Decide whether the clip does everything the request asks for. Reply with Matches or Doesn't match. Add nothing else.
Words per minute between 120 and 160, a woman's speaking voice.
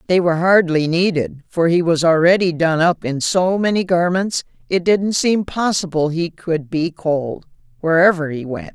Doesn't match